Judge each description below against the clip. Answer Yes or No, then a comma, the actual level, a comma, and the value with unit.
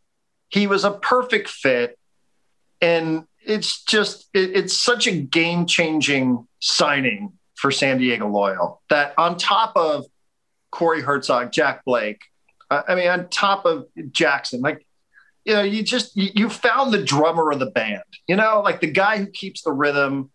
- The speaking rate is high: No, average, 160 wpm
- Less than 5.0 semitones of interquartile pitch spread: No, average, 5.3 semitones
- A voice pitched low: No, medium, 185 Hz